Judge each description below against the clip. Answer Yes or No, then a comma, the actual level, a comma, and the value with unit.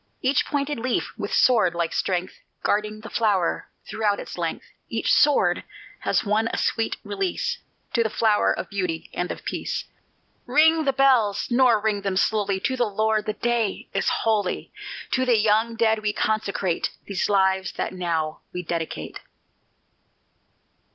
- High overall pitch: Yes, high, 215 Hz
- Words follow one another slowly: No, average, 155 wpm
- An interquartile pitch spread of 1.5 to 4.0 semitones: Yes, average, 3.4 semitones